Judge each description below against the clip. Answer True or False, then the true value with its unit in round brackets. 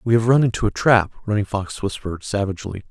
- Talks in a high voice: False (105 Hz)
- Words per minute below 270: True (205 wpm)